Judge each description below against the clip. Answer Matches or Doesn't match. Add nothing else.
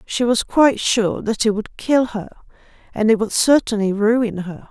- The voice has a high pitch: Matches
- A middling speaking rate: Matches